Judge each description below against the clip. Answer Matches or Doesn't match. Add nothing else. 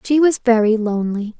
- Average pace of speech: Matches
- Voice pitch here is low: Doesn't match